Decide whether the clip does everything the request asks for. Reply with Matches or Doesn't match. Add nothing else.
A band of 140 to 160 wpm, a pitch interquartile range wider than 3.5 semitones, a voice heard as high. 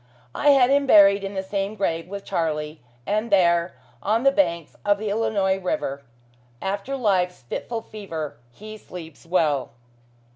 Matches